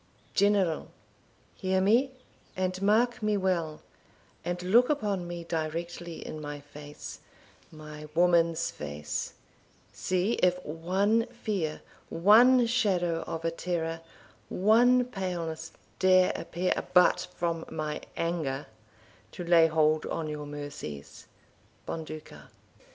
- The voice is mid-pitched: Yes, medium, 175 Hz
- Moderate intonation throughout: Yes, average, 4.0 semitones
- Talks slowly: Yes, slow, 110 wpm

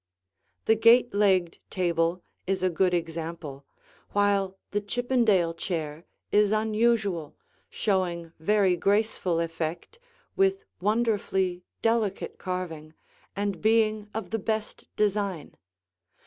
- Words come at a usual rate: No, slow, 105 wpm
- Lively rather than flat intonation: No, average, 4.0 semitones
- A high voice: Yes, high, 195 Hz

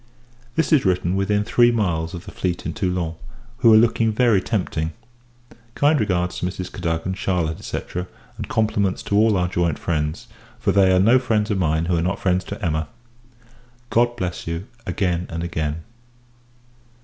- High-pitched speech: No, very low, 95 Hz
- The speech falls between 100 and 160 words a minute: No, average, 175 wpm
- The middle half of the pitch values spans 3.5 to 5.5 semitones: Yes, average, 4.1 semitones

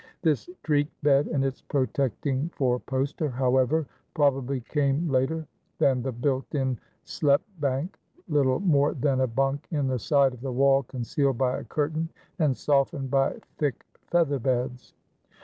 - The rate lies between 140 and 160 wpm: Yes, average, 150 wpm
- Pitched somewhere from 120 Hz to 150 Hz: Yes, low, 135 Hz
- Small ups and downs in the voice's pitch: Yes, narrow, 2.1 semitones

